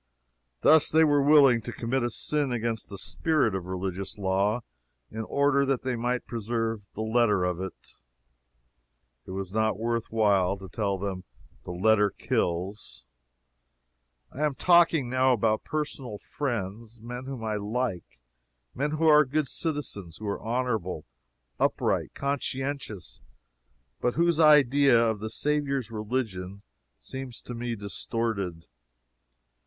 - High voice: No, low, 115 Hz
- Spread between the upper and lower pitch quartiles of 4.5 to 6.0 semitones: Yes, average, 5.1 semitones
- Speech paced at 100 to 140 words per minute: Yes, slow, 135 wpm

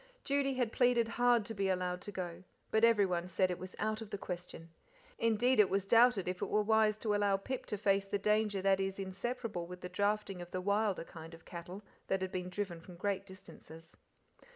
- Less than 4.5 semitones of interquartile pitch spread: Yes, average, 3.0 semitones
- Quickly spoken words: Yes, fast, 215 wpm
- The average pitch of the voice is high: Yes, high, 195 Hz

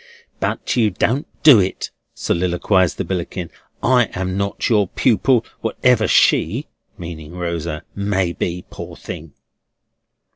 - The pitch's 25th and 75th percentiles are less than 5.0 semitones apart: Yes, average, 4.4 semitones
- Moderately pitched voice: No, very low, 95 Hz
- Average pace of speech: No, slow, 120 wpm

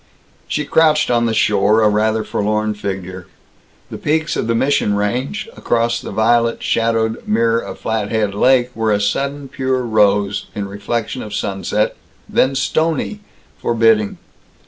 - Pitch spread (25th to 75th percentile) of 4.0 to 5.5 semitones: No, average, 3.2 semitones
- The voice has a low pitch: Yes, low, 110 Hz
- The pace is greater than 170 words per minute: No, average, 145 wpm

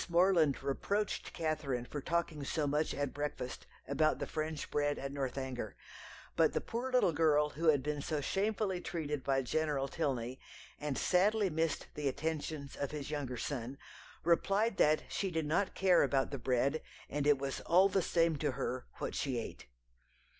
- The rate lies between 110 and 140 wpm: No, average, 170 wpm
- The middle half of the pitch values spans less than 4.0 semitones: Yes, average, 3.4 semitones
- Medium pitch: Yes, medium, 150 Hz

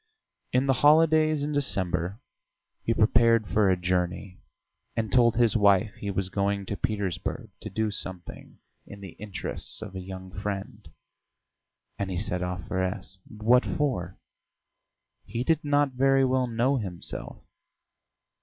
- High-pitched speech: No, low, 105 Hz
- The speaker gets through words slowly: No, average, 145 wpm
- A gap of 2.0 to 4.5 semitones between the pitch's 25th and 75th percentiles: No, average, 5.2 semitones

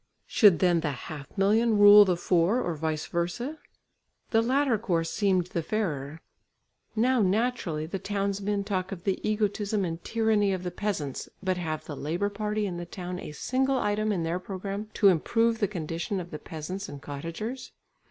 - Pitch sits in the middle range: No, high, 195 Hz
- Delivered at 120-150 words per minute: No, average, 175 wpm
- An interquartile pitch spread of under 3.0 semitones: No, average, 4.0 semitones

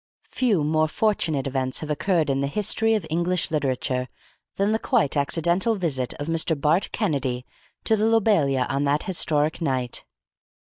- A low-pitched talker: No, medium, 155 Hz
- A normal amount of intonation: No, wide, 6.0 semitones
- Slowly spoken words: No, average, 155 wpm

